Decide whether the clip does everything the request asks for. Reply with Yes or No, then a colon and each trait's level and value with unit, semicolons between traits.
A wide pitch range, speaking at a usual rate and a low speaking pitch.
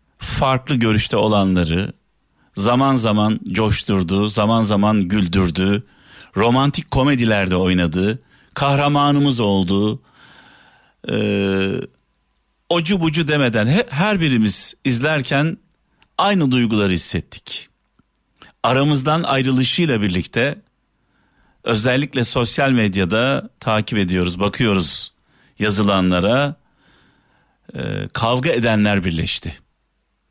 No: wide, 5.7 semitones; slow, 75 wpm; low, 110 Hz